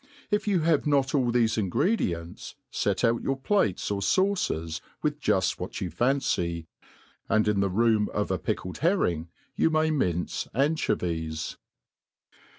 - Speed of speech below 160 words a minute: Yes, average, 145 wpm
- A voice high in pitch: No, low, 115 Hz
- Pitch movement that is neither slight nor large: No, wide, 9.0 semitones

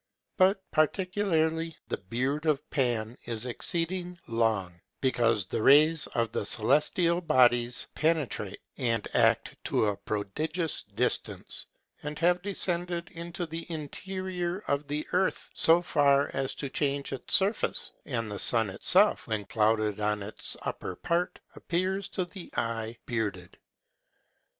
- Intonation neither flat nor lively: No, wide, 6.9 semitones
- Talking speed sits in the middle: No, slow, 130 wpm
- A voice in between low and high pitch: Yes, medium, 145 Hz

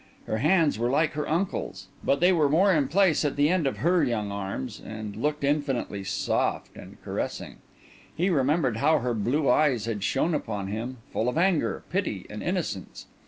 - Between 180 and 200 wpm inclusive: Yes, average, 185 wpm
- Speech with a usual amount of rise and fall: No, wide, 5.9 semitones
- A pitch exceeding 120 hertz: Yes, medium, 140 Hz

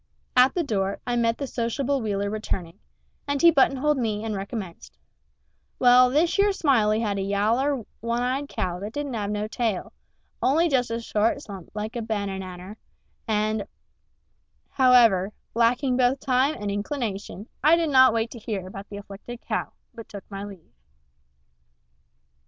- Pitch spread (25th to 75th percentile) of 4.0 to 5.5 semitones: Yes, average, 4.3 semitones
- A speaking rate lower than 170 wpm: Yes, average, 160 wpm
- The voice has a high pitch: Yes, high, 230 Hz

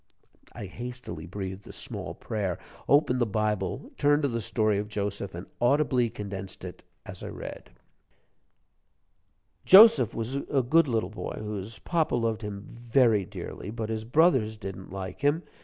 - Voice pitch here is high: No, low, 110 Hz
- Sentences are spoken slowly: No, average, 155 wpm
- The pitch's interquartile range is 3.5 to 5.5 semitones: Yes, average, 4.4 semitones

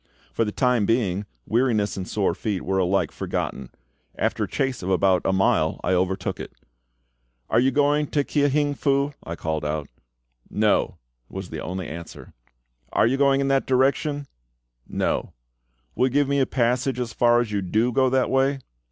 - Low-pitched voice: Yes, low, 120 Hz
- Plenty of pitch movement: Yes, wide, 6.0 semitones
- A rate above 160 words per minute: Yes, average, 180 wpm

